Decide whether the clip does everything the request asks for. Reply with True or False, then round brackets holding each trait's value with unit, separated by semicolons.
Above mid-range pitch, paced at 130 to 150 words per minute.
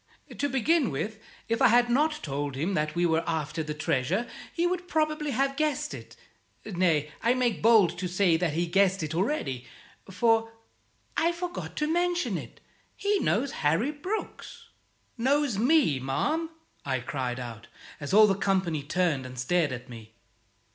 False (195 Hz; 165 wpm)